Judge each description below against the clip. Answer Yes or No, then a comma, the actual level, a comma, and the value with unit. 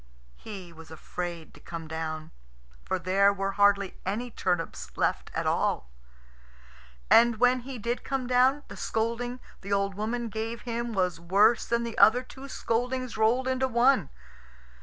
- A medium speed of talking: Yes, average, 155 wpm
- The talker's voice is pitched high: Yes, high, 220 Hz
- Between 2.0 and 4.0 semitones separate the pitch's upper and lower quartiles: No, average, 4.8 semitones